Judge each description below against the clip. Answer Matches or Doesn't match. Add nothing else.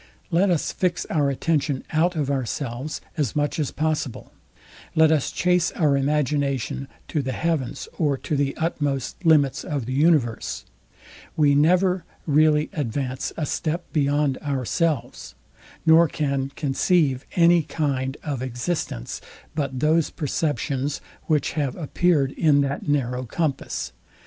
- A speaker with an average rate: Doesn't match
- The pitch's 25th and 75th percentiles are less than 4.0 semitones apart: Matches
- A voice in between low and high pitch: Matches